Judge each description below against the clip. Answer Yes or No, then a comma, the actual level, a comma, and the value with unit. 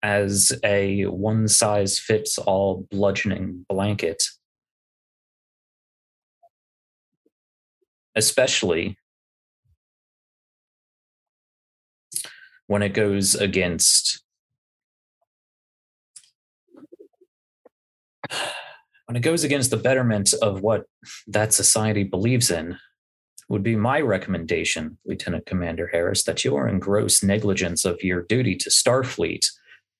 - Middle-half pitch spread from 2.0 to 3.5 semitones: Yes, average, 2.7 semitones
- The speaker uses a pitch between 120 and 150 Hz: No, low, 100 Hz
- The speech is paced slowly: Yes, slow, 90 wpm